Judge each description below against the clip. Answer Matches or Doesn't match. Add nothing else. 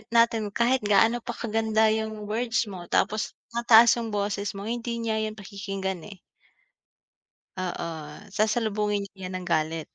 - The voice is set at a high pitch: Matches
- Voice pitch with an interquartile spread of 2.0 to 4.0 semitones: Matches